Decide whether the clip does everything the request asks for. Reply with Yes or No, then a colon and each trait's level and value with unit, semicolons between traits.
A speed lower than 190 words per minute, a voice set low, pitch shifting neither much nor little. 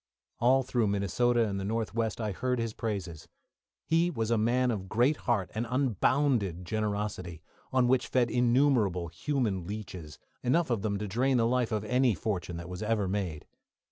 Yes: average, 175 wpm; low, 110 Hz; average, 4.1 semitones